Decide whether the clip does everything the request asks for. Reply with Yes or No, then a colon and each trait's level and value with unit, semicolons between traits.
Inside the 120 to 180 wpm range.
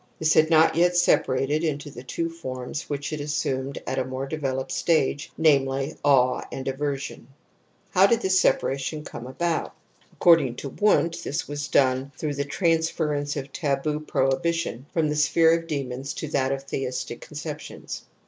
Yes: average, 165 wpm